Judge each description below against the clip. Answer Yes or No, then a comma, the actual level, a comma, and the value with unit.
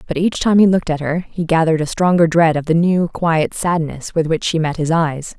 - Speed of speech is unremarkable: No, fast, 255 wpm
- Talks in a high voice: No, medium, 165 Hz